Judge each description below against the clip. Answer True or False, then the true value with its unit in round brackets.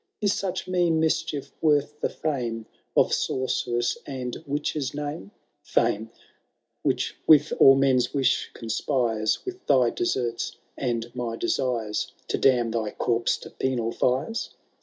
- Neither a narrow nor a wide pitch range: True (4.1 semitones)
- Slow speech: True (130 wpm)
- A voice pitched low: True (130 Hz)